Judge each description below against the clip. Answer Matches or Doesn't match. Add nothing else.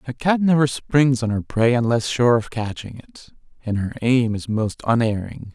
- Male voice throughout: Matches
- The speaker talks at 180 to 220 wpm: Matches